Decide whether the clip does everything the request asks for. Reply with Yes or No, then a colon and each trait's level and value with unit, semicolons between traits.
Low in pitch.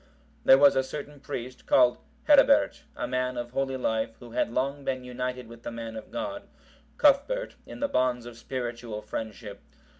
Yes: low, 125 Hz